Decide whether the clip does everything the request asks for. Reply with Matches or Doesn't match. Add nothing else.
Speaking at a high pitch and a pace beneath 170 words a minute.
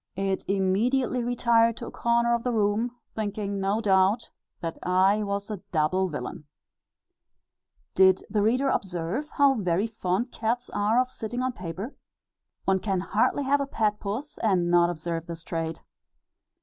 Matches